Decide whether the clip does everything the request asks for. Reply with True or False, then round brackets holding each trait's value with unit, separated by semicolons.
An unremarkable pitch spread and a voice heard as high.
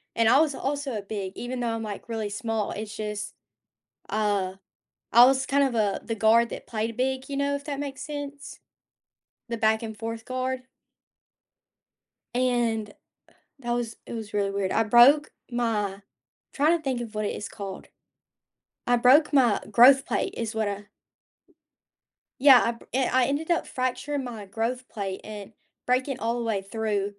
True (3.5 semitones; 235 Hz)